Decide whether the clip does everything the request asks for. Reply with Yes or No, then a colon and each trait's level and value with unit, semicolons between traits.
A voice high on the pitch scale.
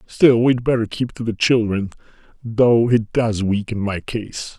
No: low, 115 Hz